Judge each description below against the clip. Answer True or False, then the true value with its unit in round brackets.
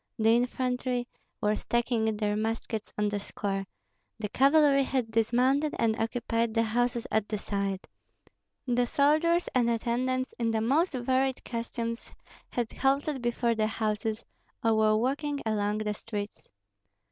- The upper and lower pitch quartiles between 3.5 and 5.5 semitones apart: False (2.9 semitones)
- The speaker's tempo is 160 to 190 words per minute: False (140 wpm)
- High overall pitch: True (230 Hz)